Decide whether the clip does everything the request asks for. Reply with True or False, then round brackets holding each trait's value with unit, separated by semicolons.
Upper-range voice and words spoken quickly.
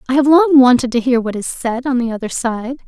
True (250 Hz; 270 wpm)